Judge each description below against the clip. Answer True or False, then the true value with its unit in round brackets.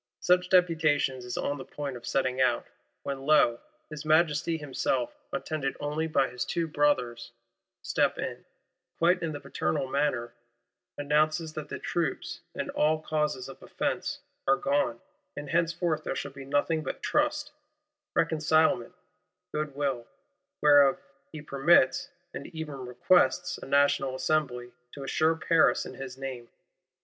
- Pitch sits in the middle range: True (145 Hz)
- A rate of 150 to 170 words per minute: False (140 wpm)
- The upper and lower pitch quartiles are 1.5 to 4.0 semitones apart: True (2.9 semitones)